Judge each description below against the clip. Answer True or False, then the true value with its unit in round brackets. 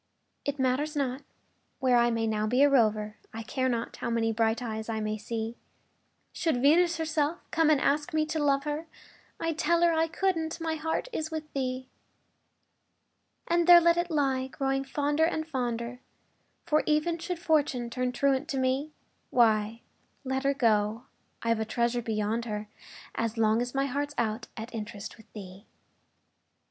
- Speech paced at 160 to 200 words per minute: True (170 wpm)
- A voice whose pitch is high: True (260 Hz)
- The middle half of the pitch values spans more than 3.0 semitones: True (5.1 semitones)